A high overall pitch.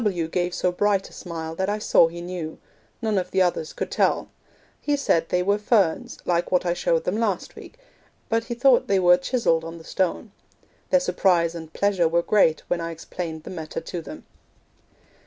No: medium, 180 Hz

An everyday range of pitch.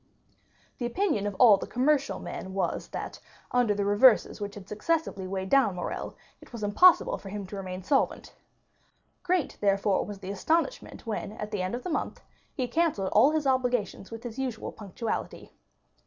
Yes: average, 5.0 semitones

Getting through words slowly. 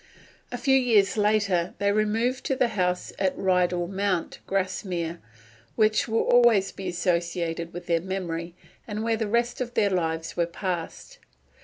No: average, 155 wpm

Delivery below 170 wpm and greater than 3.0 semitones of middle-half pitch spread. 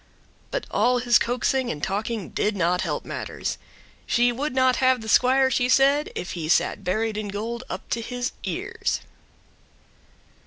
Yes: average, 160 wpm; average, 3.6 semitones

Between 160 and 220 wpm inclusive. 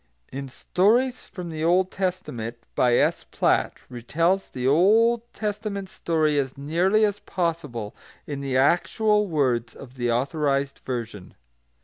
No: slow, 135 wpm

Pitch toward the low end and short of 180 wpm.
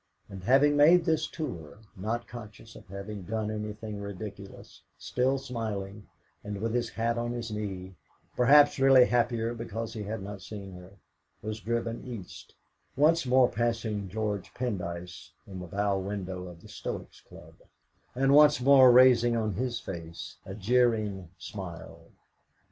Yes: low, 110 Hz; average, 150 wpm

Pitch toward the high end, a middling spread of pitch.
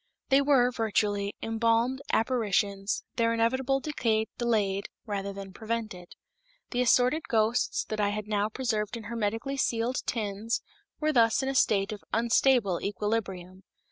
Yes: high, 225 Hz; average, 3.1 semitones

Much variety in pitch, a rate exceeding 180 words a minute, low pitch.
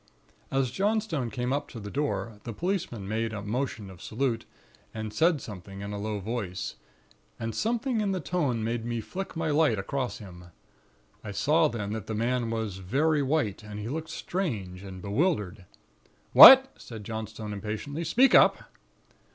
No: wide, 6.7 semitones; average, 165 wpm; low, 115 Hz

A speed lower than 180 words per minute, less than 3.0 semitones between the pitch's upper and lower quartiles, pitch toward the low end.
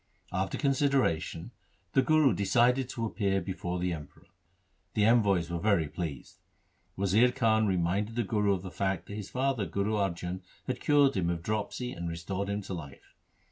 No: average, 170 wpm; average, 4.9 semitones; low, 100 Hz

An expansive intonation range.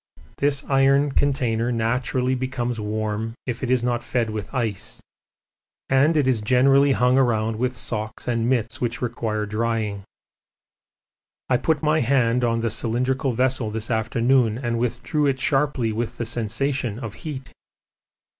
No: average, 2.8 semitones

